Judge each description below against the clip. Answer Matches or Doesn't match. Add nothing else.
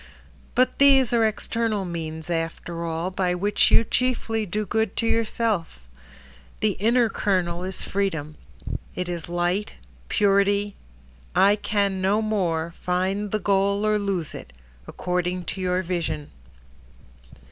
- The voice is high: Matches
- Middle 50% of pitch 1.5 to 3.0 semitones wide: Doesn't match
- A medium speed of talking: Doesn't match